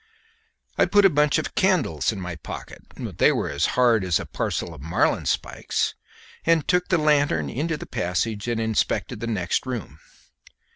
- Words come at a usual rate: Yes, average, 175 wpm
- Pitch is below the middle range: Yes, low, 115 Hz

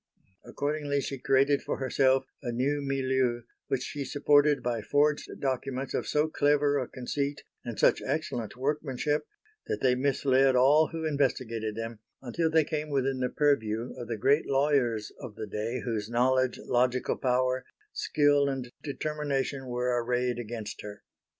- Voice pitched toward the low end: Yes, low, 130 Hz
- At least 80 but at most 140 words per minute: No, average, 150 wpm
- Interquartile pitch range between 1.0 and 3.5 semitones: Yes, average, 2.7 semitones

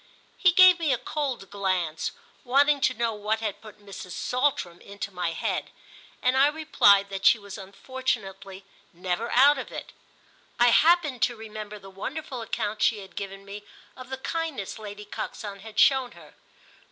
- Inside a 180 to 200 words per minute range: No, average, 165 wpm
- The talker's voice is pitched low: No, high, 220 Hz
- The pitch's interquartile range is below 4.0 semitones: No, average, 4.9 semitones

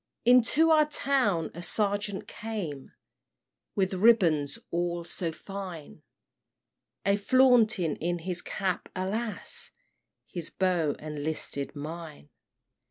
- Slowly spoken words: Yes, slow, 100 wpm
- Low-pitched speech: No, medium, 185 Hz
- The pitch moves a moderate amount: Yes, average, 5.0 semitones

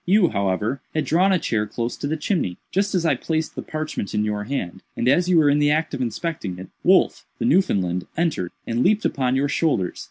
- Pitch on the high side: No, medium, 145 Hz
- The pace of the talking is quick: Yes, fast, 225 wpm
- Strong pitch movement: Yes, wide, 7.9 semitones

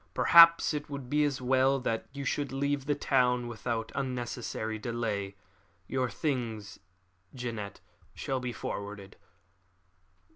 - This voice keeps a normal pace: No, slow, 120 wpm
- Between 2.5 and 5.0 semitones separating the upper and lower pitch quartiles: Yes, average, 3.5 semitones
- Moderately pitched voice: No, low, 125 Hz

